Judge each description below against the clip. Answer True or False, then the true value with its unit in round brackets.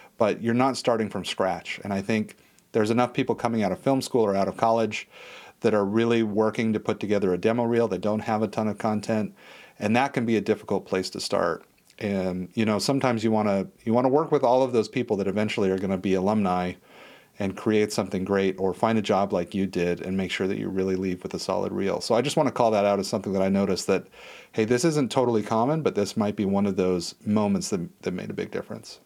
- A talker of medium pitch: False (110 Hz)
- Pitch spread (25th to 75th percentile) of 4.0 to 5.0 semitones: False (3.2 semitones)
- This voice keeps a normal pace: False (260 wpm)